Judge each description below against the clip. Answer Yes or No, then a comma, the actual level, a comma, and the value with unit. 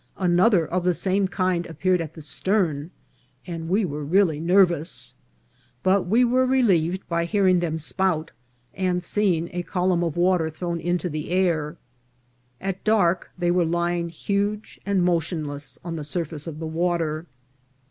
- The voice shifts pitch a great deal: No, narrow, 2.4 semitones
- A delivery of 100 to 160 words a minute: Yes, average, 155 wpm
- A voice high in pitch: No, medium, 175 Hz